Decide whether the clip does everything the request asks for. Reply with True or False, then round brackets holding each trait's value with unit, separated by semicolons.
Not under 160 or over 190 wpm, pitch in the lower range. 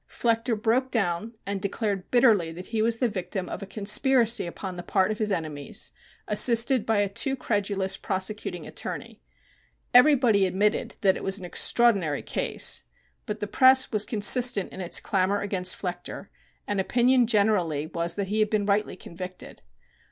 False (165 wpm; 205 Hz)